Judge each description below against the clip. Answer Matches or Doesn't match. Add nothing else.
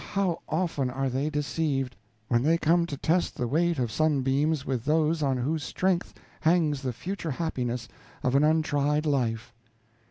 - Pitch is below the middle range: Doesn't match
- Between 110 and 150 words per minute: Doesn't match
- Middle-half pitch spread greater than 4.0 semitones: Doesn't match